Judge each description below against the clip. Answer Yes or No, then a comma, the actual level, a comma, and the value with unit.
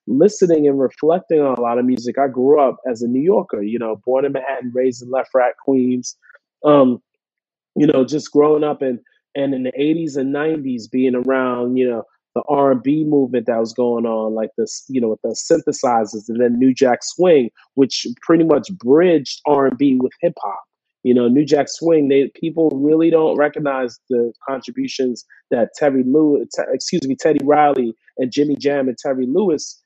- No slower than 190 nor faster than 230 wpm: Yes, average, 200 wpm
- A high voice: No, low, 135 Hz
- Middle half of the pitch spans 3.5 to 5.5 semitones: No, average, 3.0 semitones